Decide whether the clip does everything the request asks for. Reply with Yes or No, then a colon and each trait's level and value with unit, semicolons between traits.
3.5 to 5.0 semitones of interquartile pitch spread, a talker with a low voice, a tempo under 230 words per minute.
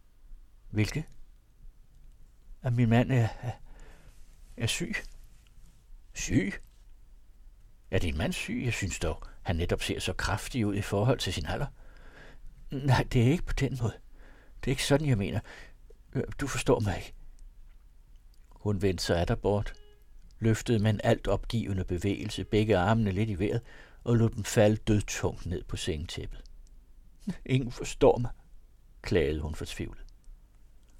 Yes: average, 3.9 semitones; low, 105 Hz; slow, 145 wpm